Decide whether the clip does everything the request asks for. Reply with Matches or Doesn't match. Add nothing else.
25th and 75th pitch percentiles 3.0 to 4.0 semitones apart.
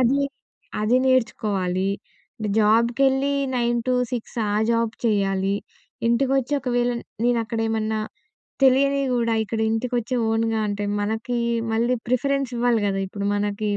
Doesn't match